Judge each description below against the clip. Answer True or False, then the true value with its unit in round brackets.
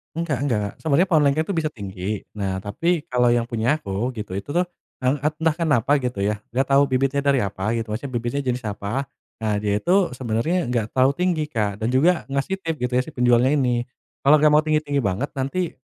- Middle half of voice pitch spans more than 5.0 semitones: True (5.4 semitones)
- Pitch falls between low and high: False (130 Hz)